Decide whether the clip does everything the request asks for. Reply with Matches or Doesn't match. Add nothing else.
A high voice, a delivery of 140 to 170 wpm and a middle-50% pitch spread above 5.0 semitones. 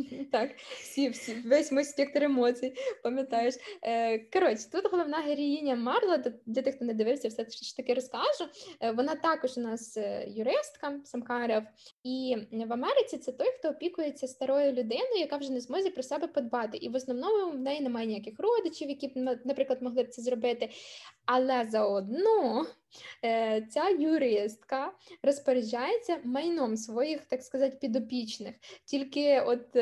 Doesn't match